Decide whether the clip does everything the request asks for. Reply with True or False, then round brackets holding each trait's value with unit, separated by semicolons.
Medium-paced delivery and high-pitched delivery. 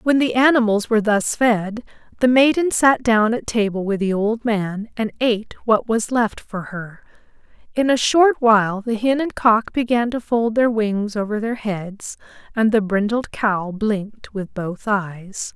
True (180 wpm; 220 Hz)